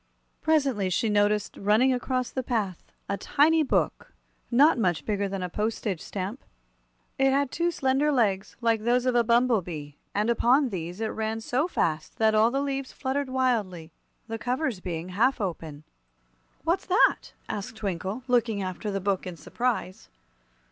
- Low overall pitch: No, high, 225 Hz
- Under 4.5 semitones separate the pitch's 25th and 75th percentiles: No, average, 5.1 semitones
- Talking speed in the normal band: Yes, average, 160 wpm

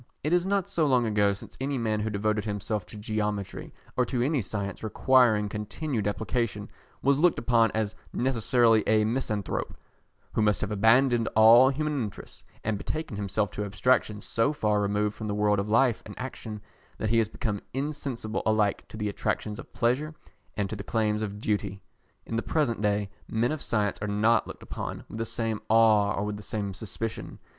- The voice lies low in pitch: Yes, low, 110 Hz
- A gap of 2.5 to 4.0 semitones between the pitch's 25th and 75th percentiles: Yes, average, 2.8 semitones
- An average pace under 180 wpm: No, average, 190 wpm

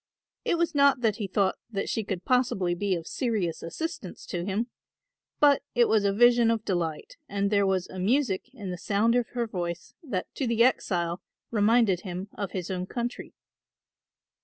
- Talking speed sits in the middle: Yes, average, 185 wpm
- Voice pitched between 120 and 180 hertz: No, high, 205 Hz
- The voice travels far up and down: No, average, 4.5 semitones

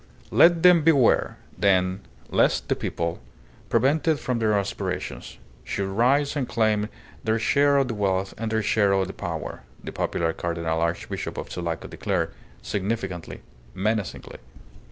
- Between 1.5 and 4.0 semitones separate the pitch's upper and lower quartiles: No, average, 5.2 semitones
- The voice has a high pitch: No, low, 105 Hz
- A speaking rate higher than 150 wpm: No, average, 140 wpm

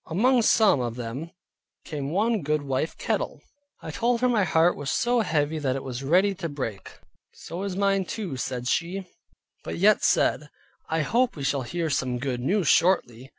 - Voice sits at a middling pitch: Yes, medium, 160 Hz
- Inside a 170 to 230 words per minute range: Yes, average, 180 wpm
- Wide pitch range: Yes, wide, 6.6 semitones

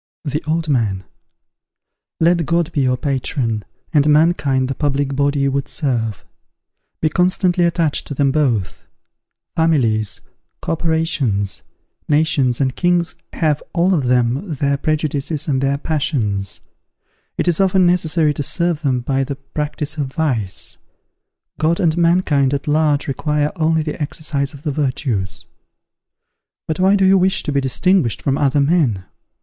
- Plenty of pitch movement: No, average, 3.5 semitones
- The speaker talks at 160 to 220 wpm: No, average, 145 wpm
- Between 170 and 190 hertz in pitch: No, medium, 145 Hz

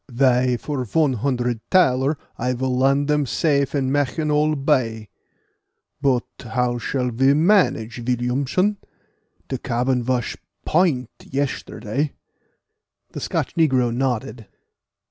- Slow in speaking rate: Yes, slow, 110 wpm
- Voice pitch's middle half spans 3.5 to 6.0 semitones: No, average, 2.7 semitones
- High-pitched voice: No, low, 130 Hz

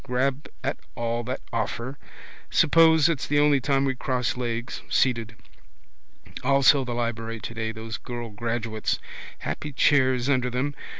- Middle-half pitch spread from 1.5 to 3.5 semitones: Yes, average, 3.0 semitones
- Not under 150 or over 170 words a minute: No, slow, 135 wpm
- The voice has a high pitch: No, low, 125 Hz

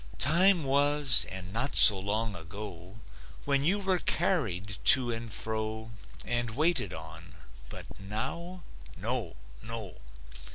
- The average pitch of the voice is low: Yes, low, 115 Hz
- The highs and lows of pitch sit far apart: Yes, wide, 6.4 semitones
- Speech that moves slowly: Yes, slow, 120 wpm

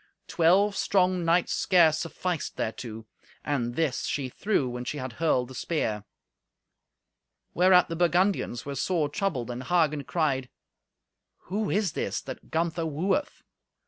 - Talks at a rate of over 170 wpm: No, slow, 135 wpm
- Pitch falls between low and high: Yes, medium, 160 Hz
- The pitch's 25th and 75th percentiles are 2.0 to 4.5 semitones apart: No, wide, 5.6 semitones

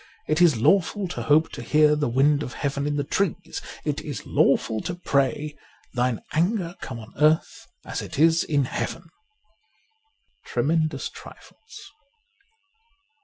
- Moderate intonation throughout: Yes, average, 3.3 semitones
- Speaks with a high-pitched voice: No, medium, 150 Hz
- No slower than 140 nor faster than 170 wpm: Yes, average, 150 wpm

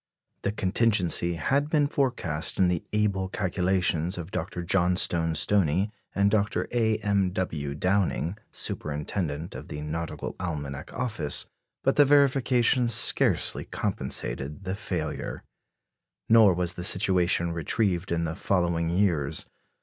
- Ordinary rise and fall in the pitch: Yes, average, 3.9 semitones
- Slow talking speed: Yes, slow, 125 wpm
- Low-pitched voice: Yes, very low, 90 Hz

